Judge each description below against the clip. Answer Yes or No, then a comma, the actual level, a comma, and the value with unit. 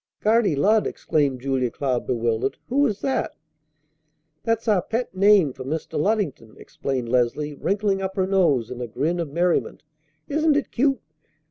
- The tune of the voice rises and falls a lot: Yes, wide, 8.2 semitones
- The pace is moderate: Yes, average, 155 wpm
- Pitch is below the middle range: No, medium, 175 Hz